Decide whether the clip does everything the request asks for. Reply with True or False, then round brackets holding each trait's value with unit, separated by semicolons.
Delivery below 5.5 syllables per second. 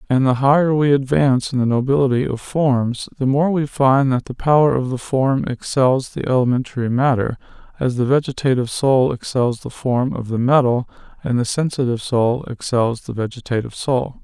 True (5.3 syllables/s)